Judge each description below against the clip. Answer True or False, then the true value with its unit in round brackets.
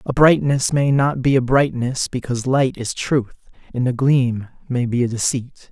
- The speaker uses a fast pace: False (190 wpm)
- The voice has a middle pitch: False (130 Hz)